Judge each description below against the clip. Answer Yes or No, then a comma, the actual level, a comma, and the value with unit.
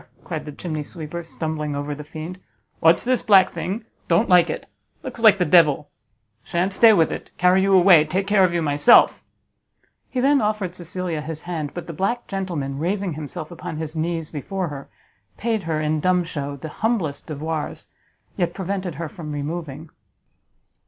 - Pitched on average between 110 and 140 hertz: No, medium, 170 Hz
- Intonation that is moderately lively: Yes, average, 3.8 semitones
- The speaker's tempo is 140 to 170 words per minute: No, average, 180 wpm